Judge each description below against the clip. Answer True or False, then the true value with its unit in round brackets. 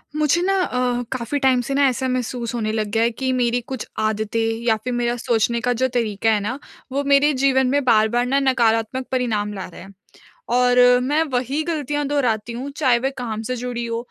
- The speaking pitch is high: True (245 Hz)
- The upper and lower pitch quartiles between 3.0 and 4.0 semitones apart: False (2.5 semitones)